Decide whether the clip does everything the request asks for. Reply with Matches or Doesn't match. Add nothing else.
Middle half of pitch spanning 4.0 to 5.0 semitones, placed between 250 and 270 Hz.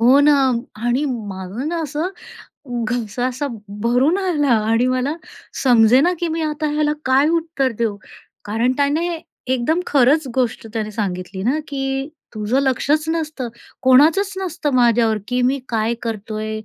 Matches